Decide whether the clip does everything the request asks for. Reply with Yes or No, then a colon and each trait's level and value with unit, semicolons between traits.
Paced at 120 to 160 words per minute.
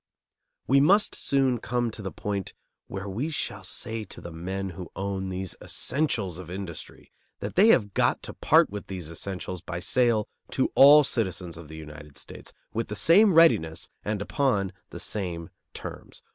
No: average, 175 wpm